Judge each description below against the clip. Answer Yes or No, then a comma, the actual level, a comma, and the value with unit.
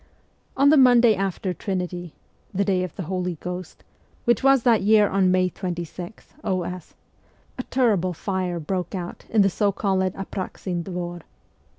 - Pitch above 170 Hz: Yes, medium, 185 Hz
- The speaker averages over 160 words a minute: No, average, 155 wpm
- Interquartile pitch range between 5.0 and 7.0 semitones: No, narrow, 2.5 semitones